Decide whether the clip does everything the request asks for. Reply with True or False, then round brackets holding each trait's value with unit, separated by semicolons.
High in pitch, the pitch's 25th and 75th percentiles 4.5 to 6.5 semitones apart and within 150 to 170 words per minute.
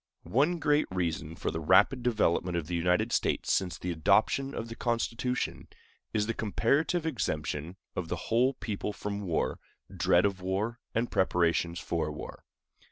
False (100 Hz; 5.6 semitones; 160 wpm)